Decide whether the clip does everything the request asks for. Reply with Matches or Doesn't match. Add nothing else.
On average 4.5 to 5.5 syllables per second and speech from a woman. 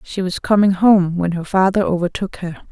Matches